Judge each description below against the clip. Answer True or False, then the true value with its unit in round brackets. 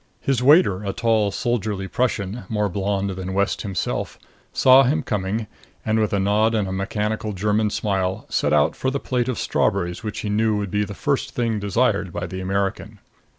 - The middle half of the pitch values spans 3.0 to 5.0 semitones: False (2.6 semitones)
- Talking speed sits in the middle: True (190 wpm)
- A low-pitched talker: True (105 Hz)